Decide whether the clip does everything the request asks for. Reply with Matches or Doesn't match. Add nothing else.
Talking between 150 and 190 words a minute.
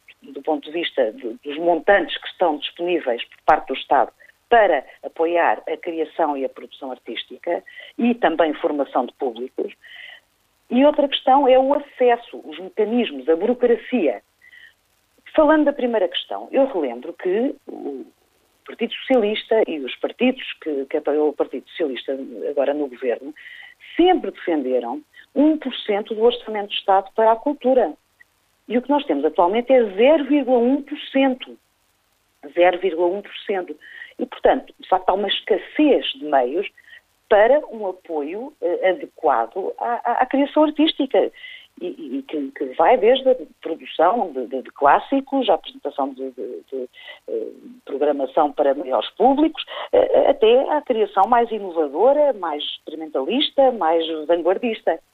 Doesn't match